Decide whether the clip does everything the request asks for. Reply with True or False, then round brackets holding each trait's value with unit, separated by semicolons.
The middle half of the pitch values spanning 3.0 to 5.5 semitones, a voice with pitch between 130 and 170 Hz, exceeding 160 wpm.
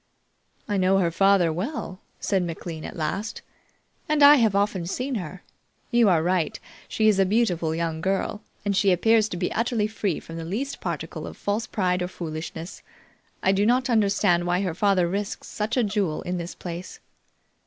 False (3.6 semitones; 195 Hz; 185 wpm)